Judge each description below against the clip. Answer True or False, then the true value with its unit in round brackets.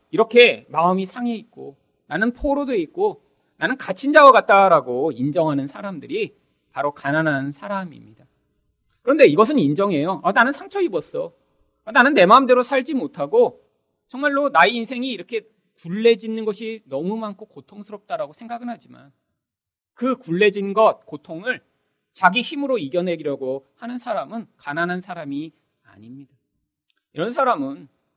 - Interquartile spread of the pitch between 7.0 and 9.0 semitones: True (7.4 semitones)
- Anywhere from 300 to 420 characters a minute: True (315 characters per minute)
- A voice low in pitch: False (215 Hz)